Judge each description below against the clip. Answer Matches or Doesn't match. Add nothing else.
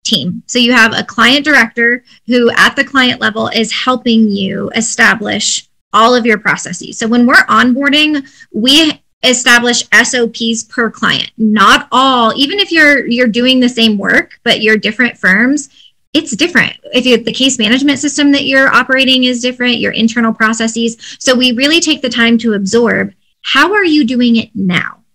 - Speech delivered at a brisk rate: Doesn't match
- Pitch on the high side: Matches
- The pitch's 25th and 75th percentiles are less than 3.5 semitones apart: Matches